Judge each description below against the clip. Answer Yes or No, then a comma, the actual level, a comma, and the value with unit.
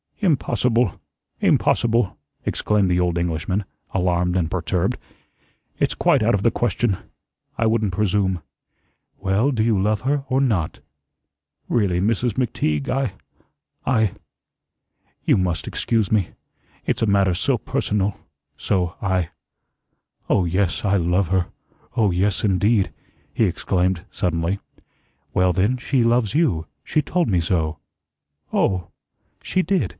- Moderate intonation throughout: Yes, average, 4.3 semitones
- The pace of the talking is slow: Yes, slow, 130 wpm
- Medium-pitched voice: No, low, 100 Hz